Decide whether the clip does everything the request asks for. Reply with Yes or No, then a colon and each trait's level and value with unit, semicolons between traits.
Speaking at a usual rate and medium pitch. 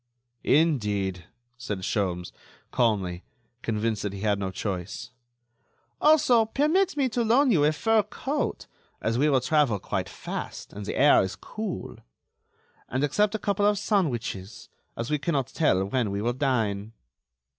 No: average, 150 wpm; low, 125 Hz